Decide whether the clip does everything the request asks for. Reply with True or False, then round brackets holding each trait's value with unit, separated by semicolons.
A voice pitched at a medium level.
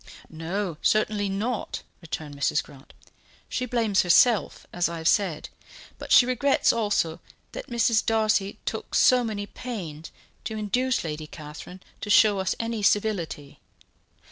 False (205 Hz)